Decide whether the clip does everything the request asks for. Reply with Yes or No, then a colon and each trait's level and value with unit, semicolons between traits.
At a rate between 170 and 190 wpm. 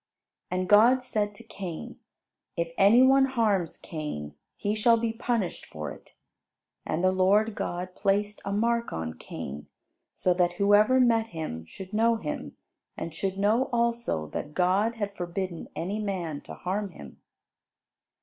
No: average, 150 wpm